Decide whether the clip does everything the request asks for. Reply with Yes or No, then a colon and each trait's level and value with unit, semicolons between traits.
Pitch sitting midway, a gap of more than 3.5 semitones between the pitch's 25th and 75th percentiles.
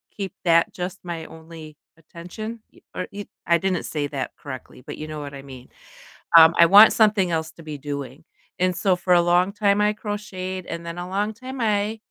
Yes: medium, 180 Hz; average, 4.1 semitones